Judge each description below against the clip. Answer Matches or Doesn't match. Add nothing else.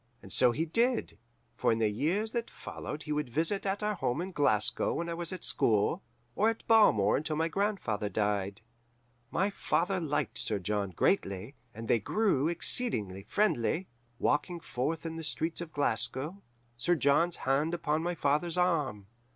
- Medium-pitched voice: Matches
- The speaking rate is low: Doesn't match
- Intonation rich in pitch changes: Matches